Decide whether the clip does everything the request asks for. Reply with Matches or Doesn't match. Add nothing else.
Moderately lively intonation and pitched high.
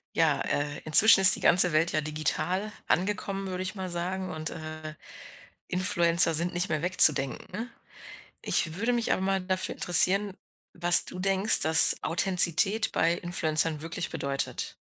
Doesn't match